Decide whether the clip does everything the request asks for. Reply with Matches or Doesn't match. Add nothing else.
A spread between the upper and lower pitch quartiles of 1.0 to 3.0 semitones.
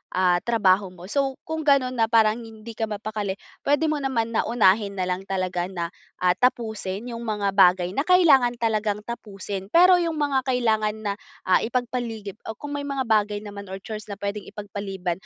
Doesn't match